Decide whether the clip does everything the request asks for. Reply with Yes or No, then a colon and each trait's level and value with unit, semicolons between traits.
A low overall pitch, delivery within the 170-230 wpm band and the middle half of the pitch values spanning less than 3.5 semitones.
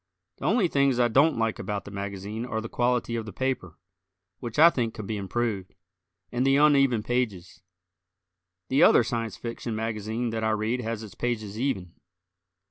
Yes: low, 115 Hz; average, 175 wpm; narrow, 2.6 semitones